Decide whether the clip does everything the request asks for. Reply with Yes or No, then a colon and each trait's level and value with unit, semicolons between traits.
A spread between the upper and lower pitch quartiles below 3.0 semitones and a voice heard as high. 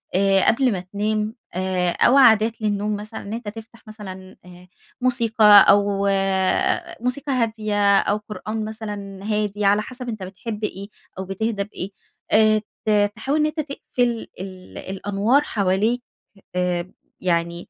Yes: narrow, 2.4 semitones; high, 210 Hz